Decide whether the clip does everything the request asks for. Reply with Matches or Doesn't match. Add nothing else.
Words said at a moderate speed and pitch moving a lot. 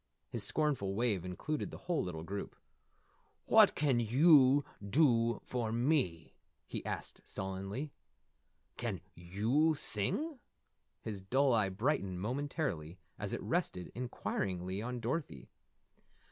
Doesn't match